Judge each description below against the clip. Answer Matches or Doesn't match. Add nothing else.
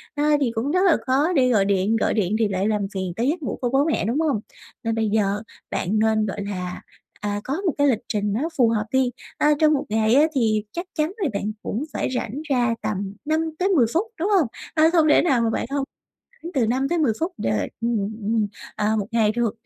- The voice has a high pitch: Matches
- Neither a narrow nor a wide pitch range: Doesn't match